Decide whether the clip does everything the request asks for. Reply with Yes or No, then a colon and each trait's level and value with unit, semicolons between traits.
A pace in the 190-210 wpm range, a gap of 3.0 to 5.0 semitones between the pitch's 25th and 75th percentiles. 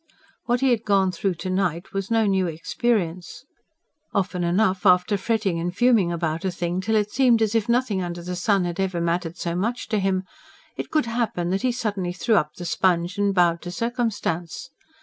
Yes: average, 200 wpm; average, 3.9 semitones